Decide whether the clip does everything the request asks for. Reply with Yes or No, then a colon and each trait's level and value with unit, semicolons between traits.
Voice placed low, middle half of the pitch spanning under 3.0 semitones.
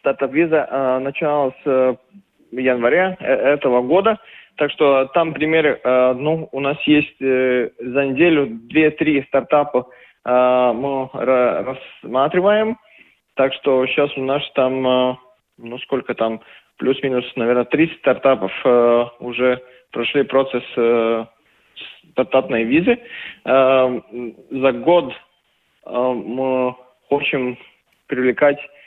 Yes: low, 130 Hz; narrow, 2.5 semitones